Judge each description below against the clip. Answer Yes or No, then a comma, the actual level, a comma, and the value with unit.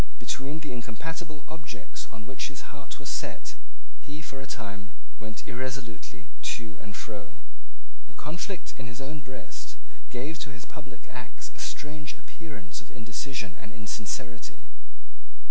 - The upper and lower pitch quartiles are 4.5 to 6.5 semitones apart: Yes, average, 5.0 semitones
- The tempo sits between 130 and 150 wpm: Yes, average, 145 wpm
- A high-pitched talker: No, low, 130 Hz